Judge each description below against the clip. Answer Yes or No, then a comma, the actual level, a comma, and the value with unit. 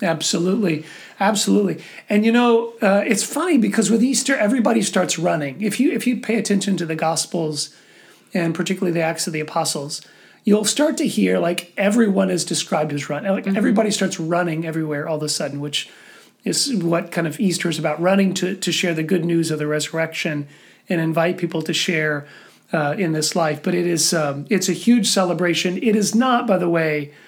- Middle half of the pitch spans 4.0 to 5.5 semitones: Yes, average, 4.3 semitones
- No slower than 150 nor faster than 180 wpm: No, average, 195 wpm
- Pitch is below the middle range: No, medium, 180 Hz